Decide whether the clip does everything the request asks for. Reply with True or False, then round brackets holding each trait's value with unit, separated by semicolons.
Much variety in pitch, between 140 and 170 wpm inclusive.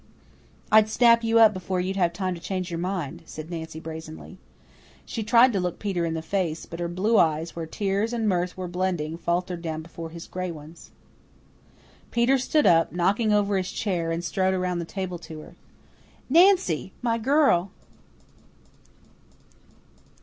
False (3.8 semitones; 165 wpm)